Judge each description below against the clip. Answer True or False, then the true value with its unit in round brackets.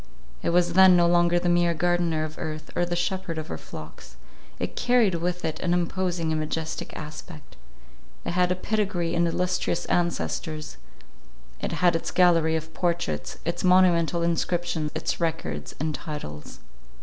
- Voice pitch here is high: False (170 Hz)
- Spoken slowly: False (160 wpm)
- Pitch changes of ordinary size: False (1.9 semitones)